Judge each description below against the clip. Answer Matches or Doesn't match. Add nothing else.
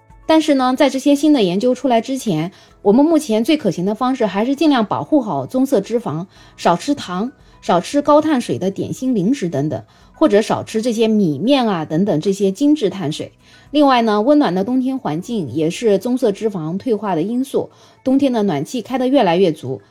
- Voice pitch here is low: Doesn't match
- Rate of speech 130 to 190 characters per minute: Doesn't match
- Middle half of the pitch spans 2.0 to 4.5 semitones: Doesn't match